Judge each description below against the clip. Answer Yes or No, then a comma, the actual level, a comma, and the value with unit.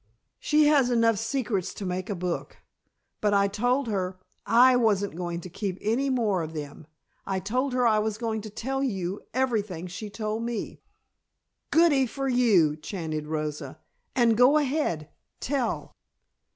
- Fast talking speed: No, average, 155 wpm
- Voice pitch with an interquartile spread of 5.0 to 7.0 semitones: Yes, wide, 5.4 semitones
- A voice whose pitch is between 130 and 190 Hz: No, high, 215 Hz